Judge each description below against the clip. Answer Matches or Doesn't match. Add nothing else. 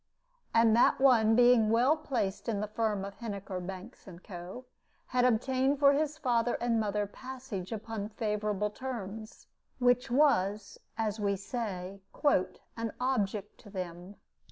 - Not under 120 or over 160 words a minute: Matches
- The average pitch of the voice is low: Doesn't match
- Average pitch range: Matches